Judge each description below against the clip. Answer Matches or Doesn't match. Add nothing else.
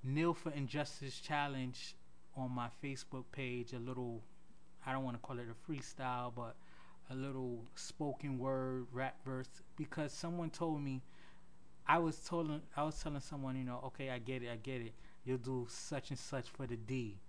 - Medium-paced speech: Matches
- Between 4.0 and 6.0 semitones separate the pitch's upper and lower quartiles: Doesn't match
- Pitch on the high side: Doesn't match